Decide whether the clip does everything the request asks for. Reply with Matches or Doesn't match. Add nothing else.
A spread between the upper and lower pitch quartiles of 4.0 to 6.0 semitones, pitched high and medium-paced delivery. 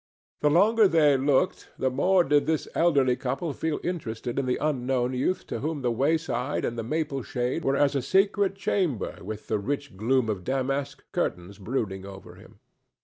Doesn't match